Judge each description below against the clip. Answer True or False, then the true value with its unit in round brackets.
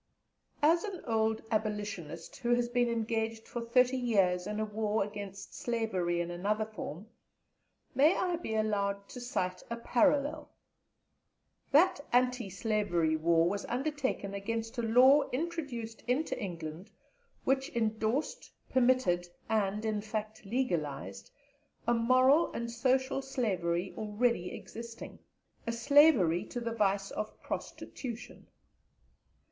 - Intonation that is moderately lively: True (4.0 semitones)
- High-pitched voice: True (225 Hz)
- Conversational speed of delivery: False (120 wpm)